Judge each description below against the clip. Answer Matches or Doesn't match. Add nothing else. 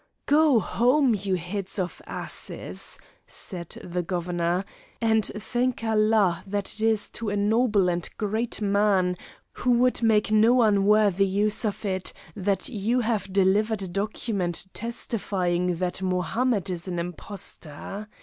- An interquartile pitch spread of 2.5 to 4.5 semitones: Matches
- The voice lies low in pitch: Doesn't match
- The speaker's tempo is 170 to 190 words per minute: Doesn't match